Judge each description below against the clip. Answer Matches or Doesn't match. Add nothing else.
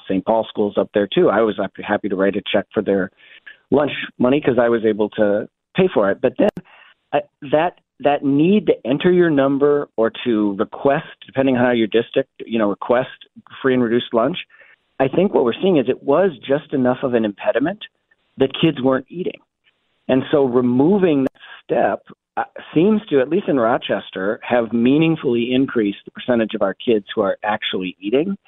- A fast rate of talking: Doesn't match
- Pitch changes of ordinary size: Matches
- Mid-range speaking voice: Doesn't match